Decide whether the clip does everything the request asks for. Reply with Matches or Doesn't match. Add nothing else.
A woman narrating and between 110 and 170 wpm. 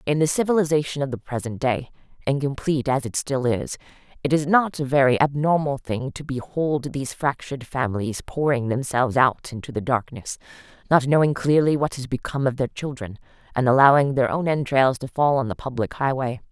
Doesn't match